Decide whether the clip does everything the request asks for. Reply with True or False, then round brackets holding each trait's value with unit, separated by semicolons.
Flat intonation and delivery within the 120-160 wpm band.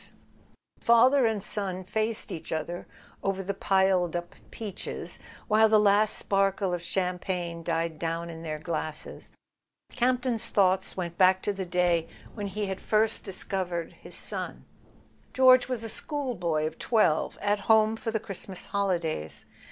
False (3.9 semitones; 150 wpm)